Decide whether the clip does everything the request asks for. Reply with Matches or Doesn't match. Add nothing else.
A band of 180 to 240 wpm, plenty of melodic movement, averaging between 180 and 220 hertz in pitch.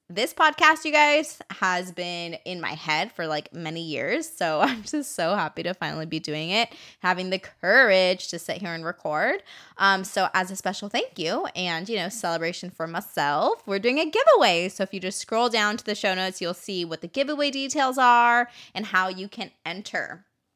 Matches